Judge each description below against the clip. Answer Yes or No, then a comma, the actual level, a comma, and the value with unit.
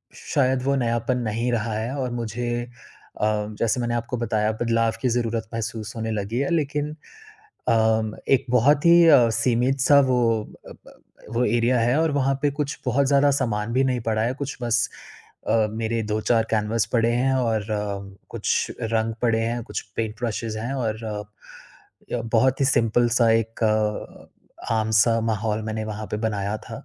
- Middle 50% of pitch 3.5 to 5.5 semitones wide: No, narrow, 2.4 semitones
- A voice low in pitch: Yes, low, 115 Hz